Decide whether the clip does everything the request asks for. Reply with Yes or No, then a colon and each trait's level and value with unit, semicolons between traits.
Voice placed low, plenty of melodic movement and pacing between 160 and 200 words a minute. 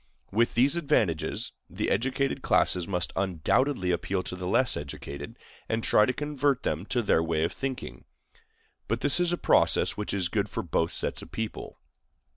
Yes: low, 105 Hz; wide, 7.0 semitones; average, 175 wpm